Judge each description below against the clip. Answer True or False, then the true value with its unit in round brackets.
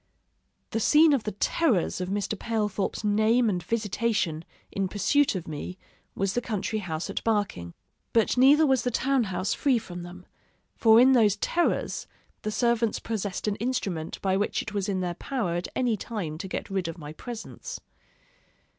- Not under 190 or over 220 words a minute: False (175 wpm)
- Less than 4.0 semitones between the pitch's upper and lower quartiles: False (4.3 semitones)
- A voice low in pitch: False (210 Hz)